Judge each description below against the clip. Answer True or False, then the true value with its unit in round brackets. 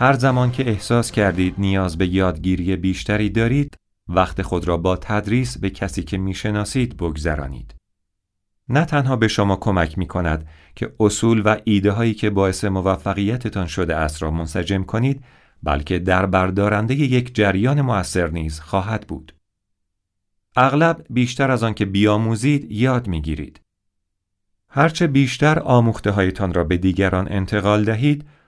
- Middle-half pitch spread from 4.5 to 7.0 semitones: False (3.7 semitones)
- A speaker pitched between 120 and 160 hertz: False (100 Hz)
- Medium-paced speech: True (140 wpm)